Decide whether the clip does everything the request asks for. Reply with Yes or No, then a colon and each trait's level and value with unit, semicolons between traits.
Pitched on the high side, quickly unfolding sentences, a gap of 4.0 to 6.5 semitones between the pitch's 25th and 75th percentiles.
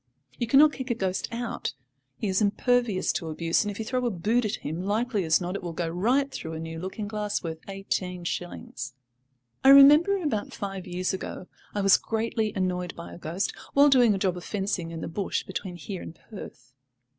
Yes: high, 195 Hz; fast, 210 wpm; average, 4.5 semitones